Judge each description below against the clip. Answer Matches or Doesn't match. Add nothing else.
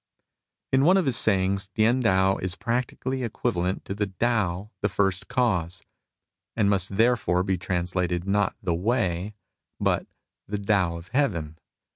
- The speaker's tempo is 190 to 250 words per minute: Doesn't match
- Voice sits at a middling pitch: Doesn't match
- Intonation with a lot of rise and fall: Doesn't match